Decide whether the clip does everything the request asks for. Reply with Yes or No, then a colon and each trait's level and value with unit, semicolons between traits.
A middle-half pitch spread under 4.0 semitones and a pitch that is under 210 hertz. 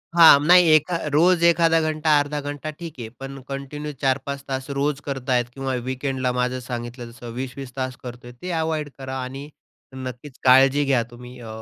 Yes: average, 2.8 semitones; low, 135 Hz